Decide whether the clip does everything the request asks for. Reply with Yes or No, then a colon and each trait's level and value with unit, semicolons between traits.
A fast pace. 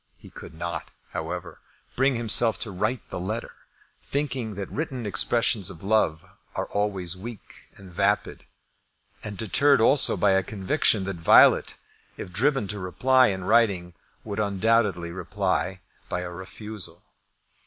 No: average, 140 wpm